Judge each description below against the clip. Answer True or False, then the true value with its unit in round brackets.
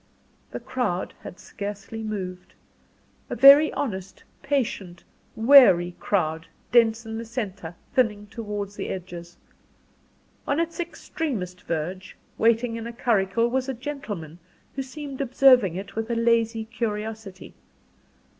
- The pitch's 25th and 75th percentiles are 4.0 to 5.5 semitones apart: True (4.6 semitones)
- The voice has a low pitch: False (220 Hz)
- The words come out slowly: True (125 wpm)